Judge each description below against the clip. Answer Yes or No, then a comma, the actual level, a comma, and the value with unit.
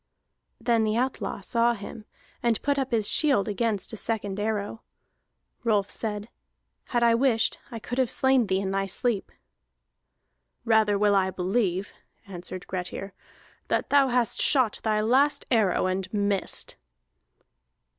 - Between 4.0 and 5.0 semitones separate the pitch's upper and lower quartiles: No, average, 3.3 semitones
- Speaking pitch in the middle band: No, high, 215 Hz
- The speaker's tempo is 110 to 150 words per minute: Yes, average, 140 wpm